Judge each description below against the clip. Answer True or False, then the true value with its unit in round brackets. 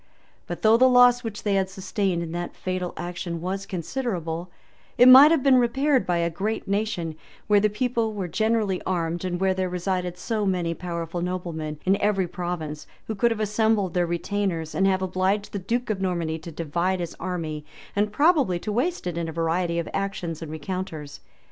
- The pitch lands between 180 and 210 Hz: True (185 Hz)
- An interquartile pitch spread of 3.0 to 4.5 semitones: True (3.7 semitones)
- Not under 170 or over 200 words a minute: True (190 wpm)